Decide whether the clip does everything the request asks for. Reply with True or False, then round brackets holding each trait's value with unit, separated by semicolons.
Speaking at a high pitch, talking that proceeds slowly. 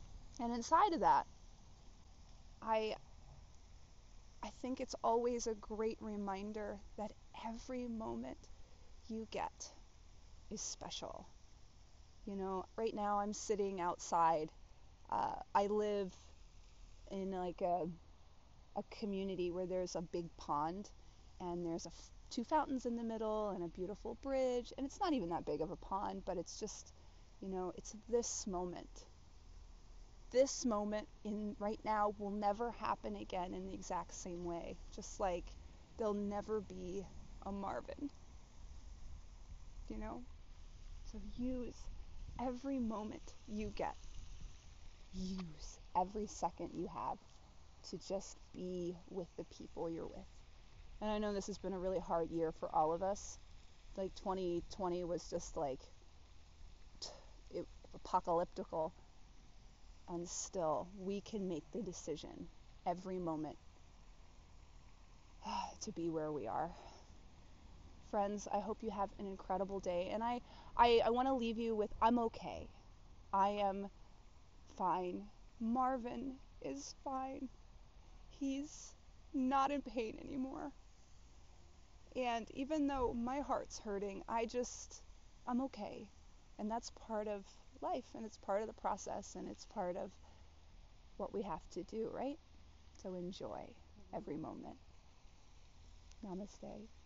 True (195 Hz; 130 wpm)